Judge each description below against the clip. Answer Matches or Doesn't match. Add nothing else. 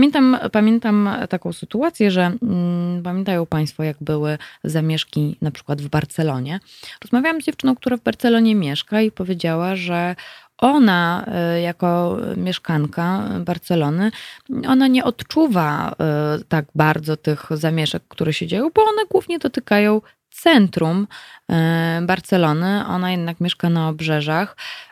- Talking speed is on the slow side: Doesn't match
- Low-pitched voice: Doesn't match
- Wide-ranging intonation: Matches